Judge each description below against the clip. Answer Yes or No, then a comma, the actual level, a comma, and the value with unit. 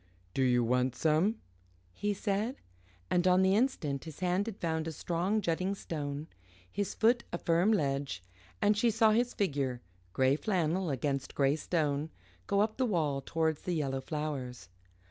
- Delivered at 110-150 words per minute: No, average, 165 wpm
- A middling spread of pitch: No, wide, 6.1 semitones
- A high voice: No, medium, 165 Hz